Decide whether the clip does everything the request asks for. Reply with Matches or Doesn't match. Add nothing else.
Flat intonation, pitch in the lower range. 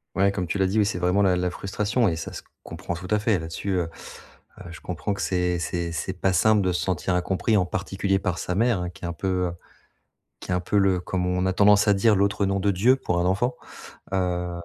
Matches